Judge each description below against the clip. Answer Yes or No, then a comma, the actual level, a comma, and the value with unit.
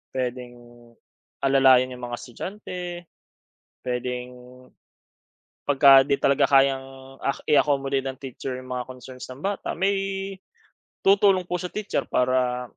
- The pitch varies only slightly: Yes, narrow, 1.8 semitones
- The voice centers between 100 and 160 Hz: Yes, low, 135 Hz